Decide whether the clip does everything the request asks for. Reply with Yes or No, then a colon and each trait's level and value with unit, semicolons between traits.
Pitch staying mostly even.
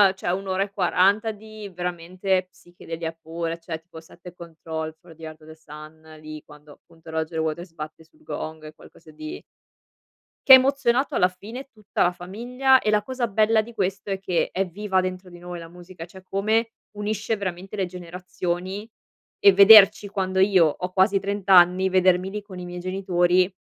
No: average, 3.0 semitones